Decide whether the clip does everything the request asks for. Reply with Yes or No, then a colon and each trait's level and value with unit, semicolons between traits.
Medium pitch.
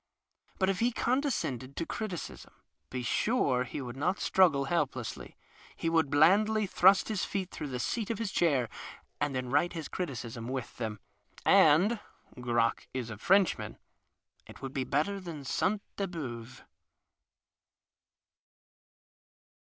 Yes: medium, 155 Hz